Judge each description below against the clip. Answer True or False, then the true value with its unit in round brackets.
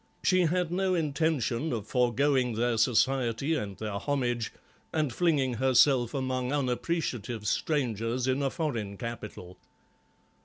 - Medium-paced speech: False (120 wpm)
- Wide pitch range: False (4.1 semitones)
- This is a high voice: False (130 Hz)